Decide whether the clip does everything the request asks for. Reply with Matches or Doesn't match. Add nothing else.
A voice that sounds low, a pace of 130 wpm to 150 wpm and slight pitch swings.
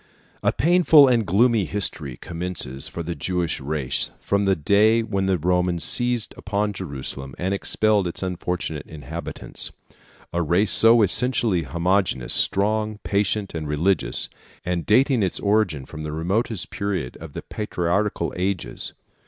Doesn't match